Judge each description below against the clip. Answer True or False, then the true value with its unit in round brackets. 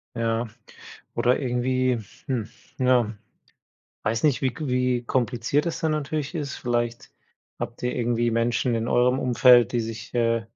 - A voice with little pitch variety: True (1.8 semitones)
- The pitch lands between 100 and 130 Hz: True (120 Hz)